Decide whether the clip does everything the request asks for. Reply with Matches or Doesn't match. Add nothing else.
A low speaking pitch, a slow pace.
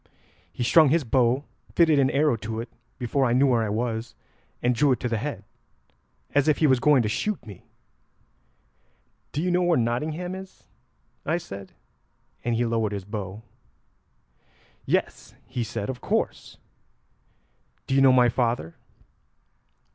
Doesn't match